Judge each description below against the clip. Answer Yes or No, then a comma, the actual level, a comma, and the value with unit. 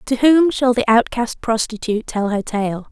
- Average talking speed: Yes, average, 185 wpm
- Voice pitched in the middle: No, high, 235 Hz